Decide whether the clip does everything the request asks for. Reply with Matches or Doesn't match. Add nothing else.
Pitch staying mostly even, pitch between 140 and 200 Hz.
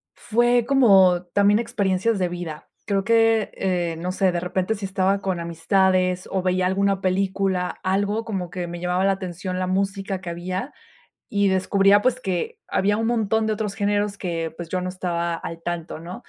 Matches